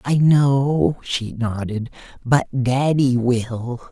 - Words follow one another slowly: Yes, slow, 105 wpm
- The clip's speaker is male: Yes, male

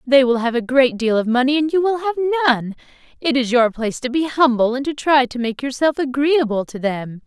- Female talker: Yes, female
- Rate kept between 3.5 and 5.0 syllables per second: No, 5.5 syllables/s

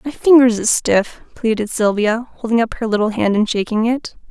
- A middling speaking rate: Yes, average, 195 wpm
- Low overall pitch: No, high, 225 Hz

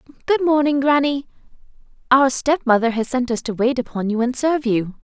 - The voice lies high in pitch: Yes, very high, 260 Hz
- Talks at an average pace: Yes, average, 190 wpm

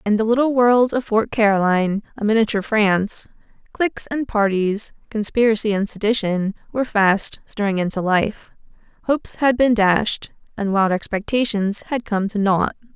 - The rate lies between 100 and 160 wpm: Yes, average, 150 wpm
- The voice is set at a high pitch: Yes, high, 215 Hz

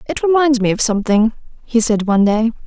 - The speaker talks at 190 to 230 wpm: Yes, average, 200 wpm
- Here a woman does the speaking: Yes, female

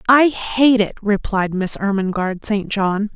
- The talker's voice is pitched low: No, high, 210 Hz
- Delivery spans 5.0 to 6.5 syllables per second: No, 4.1 syllables/s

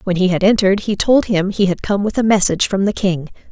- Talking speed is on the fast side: Yes, fast, 275 wpm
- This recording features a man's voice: No, female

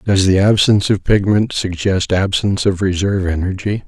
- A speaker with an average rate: Yes, average, 155 wpm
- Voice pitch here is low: Yes, very low, 95 Hz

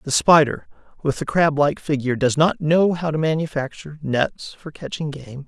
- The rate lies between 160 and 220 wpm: Yes, average, 185 wpm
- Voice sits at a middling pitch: Yes, medium, 150 Hz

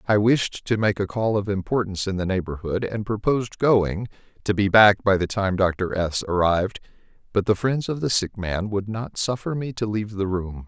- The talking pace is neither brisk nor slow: No, fast, 215 wpm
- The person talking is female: No, male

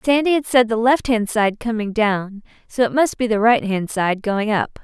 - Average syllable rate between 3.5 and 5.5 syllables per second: Yes, 4.7 syllables/s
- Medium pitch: No, high, 225 Hz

